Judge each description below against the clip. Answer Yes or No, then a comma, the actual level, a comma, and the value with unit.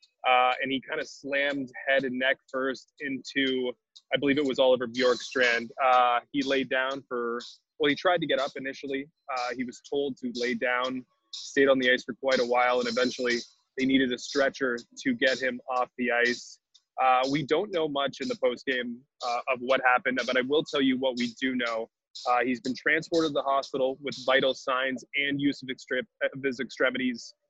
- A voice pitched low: Yes, low, 130 Hz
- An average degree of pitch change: No, narrow, 1.8 semitones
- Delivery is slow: No, fast, 205 wpm